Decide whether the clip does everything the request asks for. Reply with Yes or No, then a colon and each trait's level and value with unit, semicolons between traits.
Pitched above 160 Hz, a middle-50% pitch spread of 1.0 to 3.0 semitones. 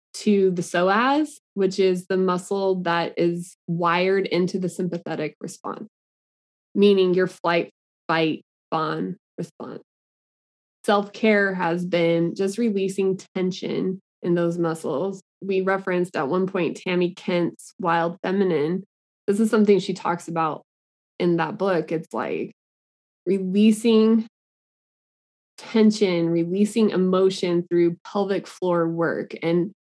Yes: medium, 185 Hz; narrow, 2.5 semitones